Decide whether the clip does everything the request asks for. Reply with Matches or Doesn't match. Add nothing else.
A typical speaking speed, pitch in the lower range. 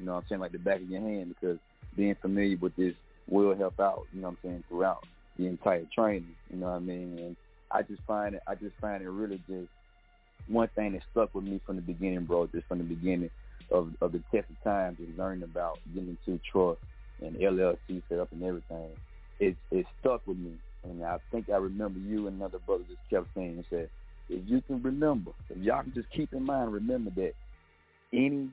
Doesn't match